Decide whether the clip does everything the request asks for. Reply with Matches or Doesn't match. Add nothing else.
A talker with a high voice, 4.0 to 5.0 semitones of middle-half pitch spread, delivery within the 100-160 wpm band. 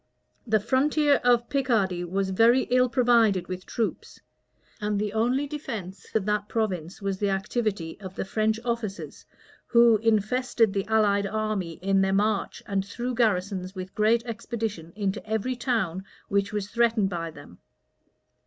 Doesn't match